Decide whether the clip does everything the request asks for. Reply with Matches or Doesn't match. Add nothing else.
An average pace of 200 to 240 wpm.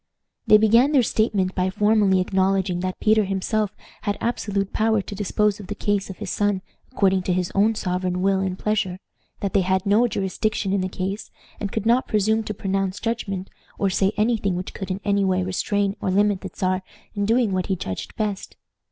Matches